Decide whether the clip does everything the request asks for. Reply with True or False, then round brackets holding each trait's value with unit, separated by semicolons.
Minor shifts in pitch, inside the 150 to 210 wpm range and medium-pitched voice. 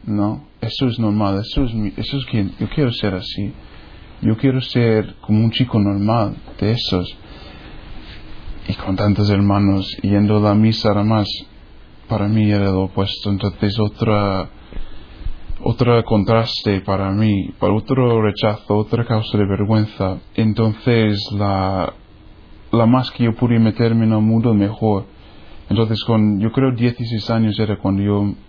False (2.2 semitones; 155 wpm; 105 Hz)